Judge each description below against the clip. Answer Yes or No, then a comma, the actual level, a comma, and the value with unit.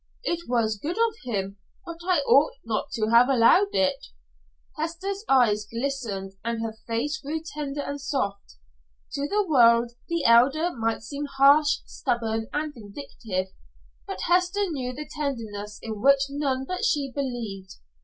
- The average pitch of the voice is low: No, very high, 270 Hz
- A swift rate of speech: No, average, 150 wpm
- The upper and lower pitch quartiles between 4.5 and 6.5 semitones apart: Yes, average, 5.1 semitones